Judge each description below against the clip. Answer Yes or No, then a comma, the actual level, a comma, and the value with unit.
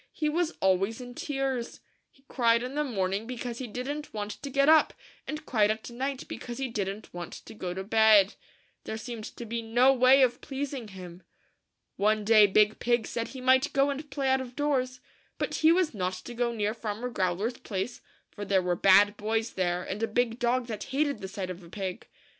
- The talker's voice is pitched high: Yes, high, 230 Hz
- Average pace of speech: No, fast, 210 wpm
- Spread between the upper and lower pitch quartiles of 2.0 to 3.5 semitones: No, average, 4.2 semitones